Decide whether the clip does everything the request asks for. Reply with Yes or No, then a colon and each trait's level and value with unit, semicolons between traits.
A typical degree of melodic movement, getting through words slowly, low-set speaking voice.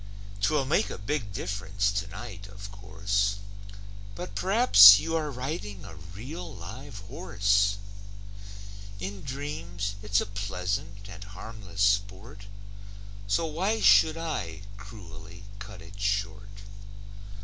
Yes: average, 3.6 semitones; slow, 115 wpm; low, 100 Hz